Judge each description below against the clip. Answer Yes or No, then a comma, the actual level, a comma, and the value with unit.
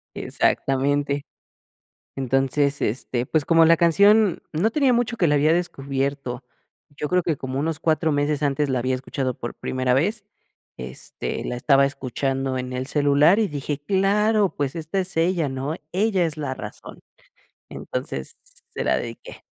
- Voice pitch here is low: No, medium, 145 Hz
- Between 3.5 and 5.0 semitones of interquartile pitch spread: Yes, average, 4.5 semitones